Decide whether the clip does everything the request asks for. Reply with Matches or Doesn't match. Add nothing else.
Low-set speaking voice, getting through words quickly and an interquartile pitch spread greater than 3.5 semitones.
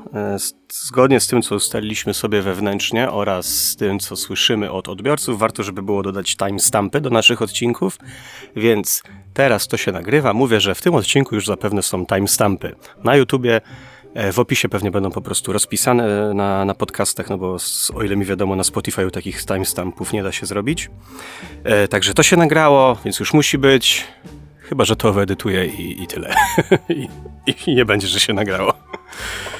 Matches